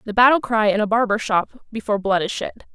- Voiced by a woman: Yes, female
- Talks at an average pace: No, fast, 240 wpm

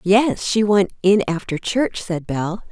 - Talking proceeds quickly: No, average, 175 wpm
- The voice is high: Yes, high, 195 Hz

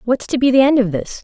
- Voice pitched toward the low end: No, high, 245 Hz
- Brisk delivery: Yes, fast, 340 wpm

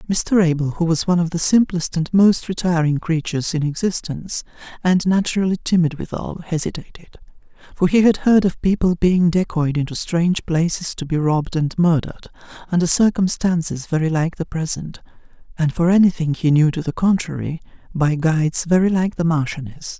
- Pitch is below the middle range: No, medium, 170 Hz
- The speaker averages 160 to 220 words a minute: Yes, average, 165 wpm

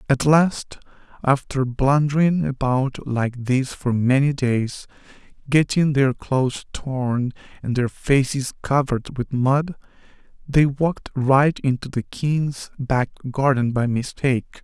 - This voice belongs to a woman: No, male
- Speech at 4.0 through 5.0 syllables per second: No, 3.8 syllables/s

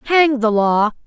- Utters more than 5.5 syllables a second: No, 3.8 syllables/s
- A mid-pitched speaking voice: No, high, 245 Hz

